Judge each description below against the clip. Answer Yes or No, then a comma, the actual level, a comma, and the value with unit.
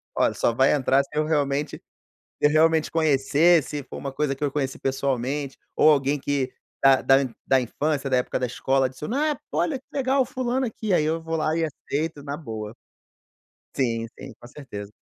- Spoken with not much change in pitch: No, average, 3.2 semitones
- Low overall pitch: No, medium, 145 Hz